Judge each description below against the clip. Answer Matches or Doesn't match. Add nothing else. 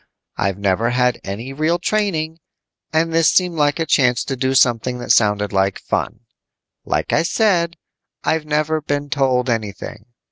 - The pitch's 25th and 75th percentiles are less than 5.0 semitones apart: Doesn't match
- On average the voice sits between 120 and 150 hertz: Matches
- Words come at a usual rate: Matches